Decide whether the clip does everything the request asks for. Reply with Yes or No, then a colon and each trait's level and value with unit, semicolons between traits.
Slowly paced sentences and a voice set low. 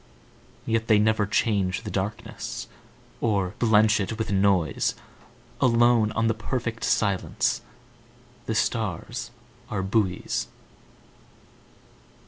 Yes: slow, 85 wpm; low, 110 Hz